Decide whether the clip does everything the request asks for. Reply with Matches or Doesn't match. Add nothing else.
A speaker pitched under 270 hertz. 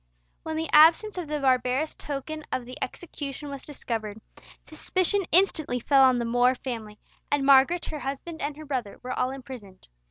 Doesn't match